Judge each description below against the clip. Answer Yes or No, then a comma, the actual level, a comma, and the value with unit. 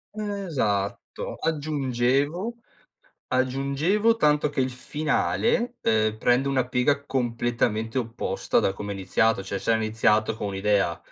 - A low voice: Yes, low, 130 Hz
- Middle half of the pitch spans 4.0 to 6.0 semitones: Yes, average, 5.2 semitones